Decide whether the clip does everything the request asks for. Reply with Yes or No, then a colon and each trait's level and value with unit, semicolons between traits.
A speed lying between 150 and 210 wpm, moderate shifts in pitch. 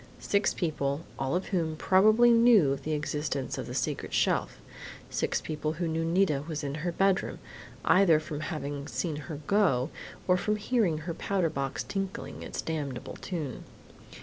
Yes: average, 165 wpm; average, 4.4 semitones